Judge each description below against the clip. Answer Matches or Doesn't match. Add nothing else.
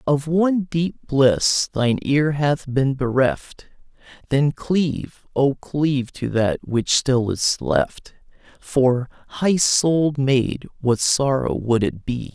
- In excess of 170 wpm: Doesn't match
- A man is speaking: Matches